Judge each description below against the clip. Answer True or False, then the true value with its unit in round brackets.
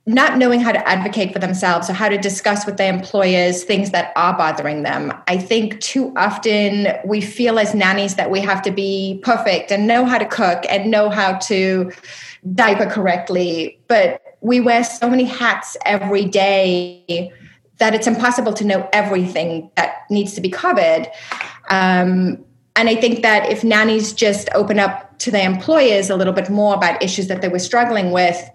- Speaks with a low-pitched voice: False (200 Hz)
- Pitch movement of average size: True (3.1 semitones)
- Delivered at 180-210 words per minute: True (185 wpm)